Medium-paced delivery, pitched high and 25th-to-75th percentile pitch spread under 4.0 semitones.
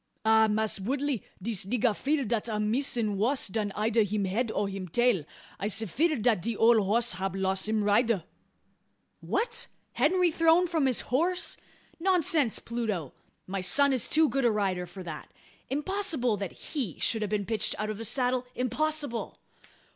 No: average, 170 wpm; high, 230 Hz; average, 5.0 semitones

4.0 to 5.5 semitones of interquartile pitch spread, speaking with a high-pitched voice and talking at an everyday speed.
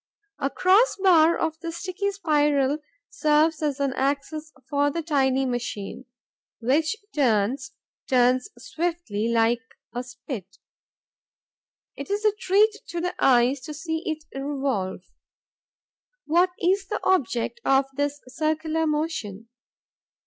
No: average, 4.5 semitones; very high, 295 Hz; slow, 120 wpm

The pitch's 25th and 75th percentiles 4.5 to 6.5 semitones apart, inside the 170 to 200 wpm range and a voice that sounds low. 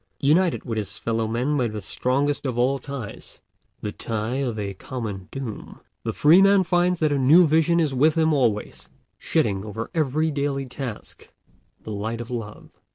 Yes: average, 5.2 semitones; average, 175 wpm; low, 130 Hz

